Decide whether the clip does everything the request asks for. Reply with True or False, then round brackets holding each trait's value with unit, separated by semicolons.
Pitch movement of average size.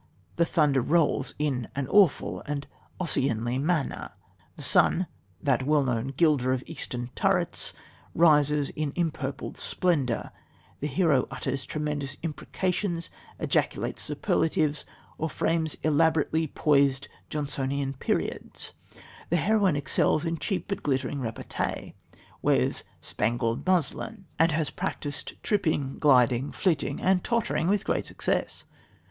True (3.6 semitones)